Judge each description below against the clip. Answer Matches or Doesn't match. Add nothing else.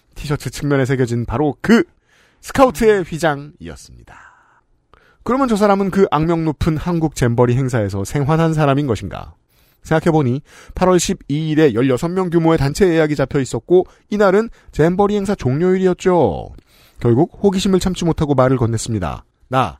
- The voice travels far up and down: Matches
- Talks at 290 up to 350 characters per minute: Matches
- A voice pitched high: Doesn't match